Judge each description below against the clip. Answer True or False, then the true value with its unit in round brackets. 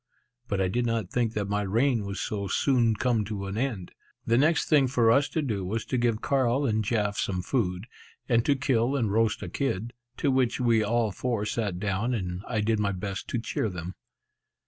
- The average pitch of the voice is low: True (115 Hz)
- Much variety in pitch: False (3.6 semitones)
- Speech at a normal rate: False (215 wpm)